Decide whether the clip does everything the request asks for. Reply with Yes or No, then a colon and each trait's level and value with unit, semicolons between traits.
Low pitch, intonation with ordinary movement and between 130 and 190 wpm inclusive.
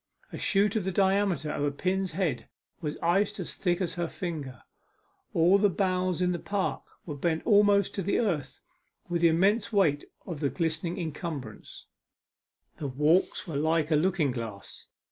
No: medium, 175 Hz; average, 4.0 semitones; average, 170 wpm